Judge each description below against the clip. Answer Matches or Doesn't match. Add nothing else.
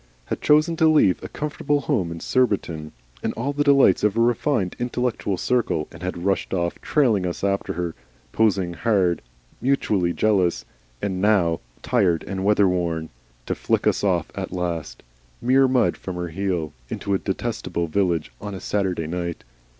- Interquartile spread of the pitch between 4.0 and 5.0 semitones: Doesn't match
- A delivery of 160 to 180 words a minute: Matches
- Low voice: Matches